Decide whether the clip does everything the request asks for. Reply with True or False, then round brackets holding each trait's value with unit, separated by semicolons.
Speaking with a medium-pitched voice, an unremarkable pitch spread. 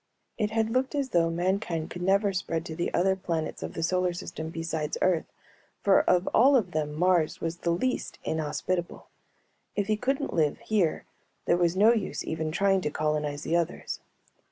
True (175 Hz; 3.7 semitones)